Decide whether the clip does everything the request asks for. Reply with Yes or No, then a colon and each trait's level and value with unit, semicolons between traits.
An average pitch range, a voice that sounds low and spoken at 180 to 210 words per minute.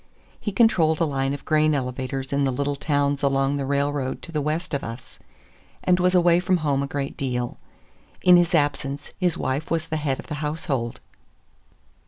No: average, 3.1 semitones; medium, 145 Hz; average, 190 wpm